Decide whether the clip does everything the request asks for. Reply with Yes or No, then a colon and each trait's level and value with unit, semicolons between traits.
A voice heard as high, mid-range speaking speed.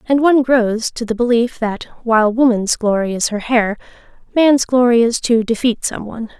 Yes: high, 235 Hz; average, 190 wpm